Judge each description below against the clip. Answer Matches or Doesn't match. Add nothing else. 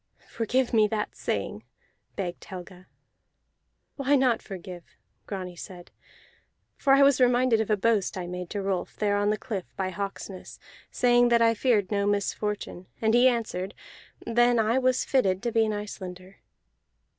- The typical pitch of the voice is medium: Doesn't match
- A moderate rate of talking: Matches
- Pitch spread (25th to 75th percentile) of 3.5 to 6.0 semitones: Matches